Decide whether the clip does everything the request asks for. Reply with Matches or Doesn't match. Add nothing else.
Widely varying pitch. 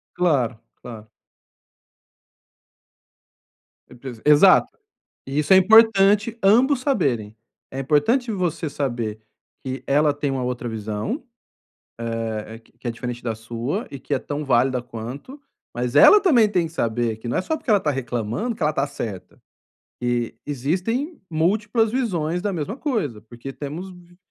Matches